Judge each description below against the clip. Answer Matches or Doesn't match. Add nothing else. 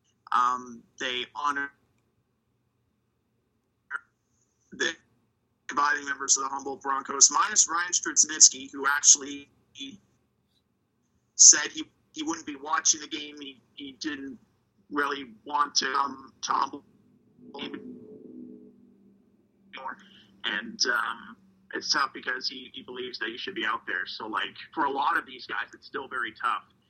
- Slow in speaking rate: Matches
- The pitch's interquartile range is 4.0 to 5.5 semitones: Matches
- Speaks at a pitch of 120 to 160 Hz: Matches